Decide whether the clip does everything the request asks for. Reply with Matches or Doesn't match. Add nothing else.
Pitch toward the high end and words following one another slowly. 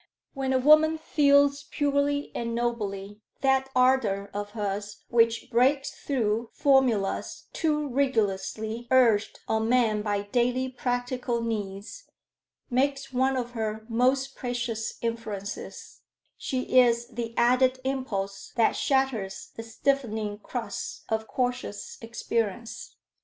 Matches